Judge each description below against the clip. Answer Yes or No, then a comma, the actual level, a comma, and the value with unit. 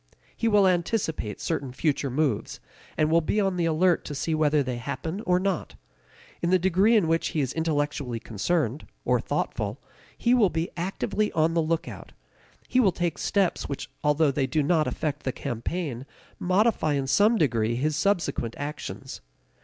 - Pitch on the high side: No, medium, 160 Hz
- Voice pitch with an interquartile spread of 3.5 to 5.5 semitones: Yes, average, 4.4 semitones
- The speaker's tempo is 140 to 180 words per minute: Yes, average, 170 wpm